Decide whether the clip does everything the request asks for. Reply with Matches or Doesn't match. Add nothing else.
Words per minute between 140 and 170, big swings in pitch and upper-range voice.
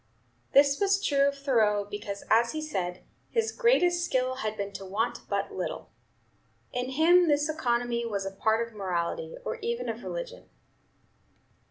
Matches